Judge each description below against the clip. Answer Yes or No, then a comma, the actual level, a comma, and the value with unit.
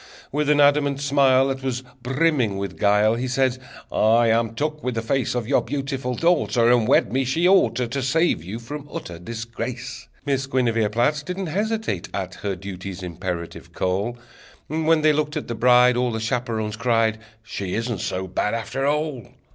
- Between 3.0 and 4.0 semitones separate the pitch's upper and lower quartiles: No, average, 4.4 semitones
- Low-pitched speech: Yes, low, 125 Hz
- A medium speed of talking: Yes, average, 180 wpm